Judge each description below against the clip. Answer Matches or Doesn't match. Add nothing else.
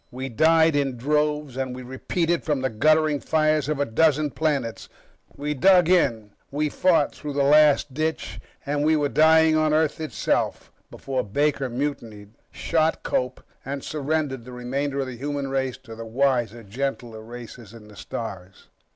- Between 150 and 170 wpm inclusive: Matches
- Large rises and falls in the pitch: Doesn't match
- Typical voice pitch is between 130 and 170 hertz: Matches